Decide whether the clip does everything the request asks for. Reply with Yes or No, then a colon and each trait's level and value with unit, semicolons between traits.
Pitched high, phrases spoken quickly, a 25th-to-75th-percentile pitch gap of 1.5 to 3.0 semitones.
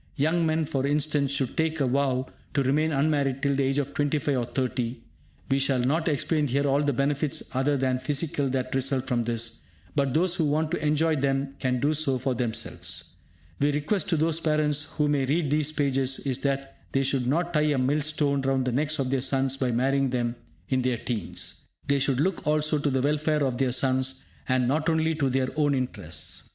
No: medium, 140 Hz; fast, 210 wpm; narrow, 2.4 semitones